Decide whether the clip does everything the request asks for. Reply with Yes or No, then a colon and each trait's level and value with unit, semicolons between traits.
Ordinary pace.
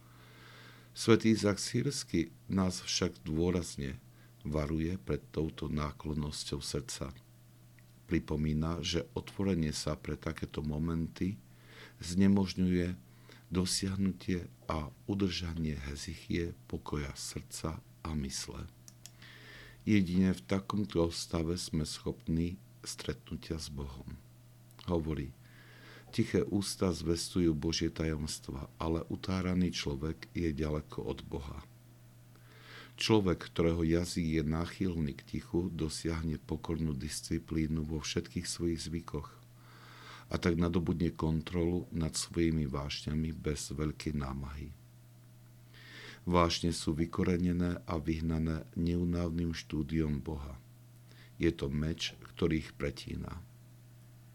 No: slow, 95 wpm